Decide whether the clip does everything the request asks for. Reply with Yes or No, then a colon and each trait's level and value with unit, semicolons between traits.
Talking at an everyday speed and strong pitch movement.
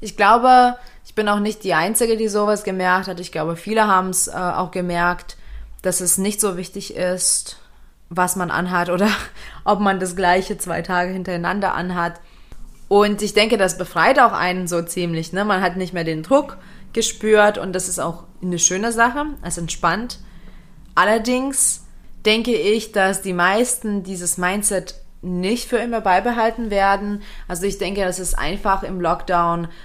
No: average, 170 wpm; average, 2.9 semitones